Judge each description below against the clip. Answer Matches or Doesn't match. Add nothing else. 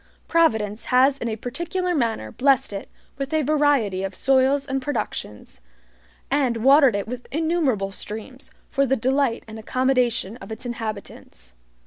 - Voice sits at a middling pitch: Doesn't match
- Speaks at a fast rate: Doesn't match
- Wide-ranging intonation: Doesn't match